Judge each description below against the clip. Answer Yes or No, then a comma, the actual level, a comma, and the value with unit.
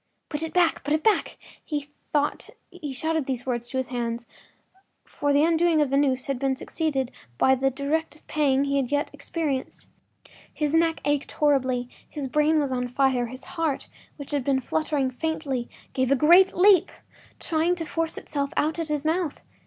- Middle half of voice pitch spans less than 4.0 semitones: Yes, average, 3.3 semitones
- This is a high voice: Yes, very high, 290 Hz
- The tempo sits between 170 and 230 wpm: Yes, average, 185 wpm